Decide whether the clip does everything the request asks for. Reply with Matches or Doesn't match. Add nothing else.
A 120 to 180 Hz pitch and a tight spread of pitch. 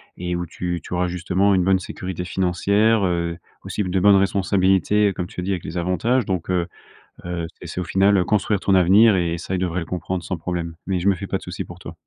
Doesn't match